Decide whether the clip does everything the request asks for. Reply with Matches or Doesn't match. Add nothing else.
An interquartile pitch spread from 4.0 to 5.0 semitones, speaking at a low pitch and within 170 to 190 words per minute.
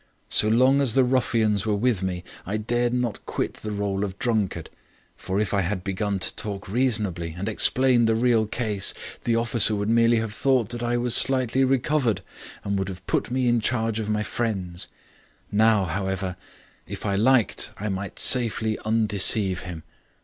Doesn't match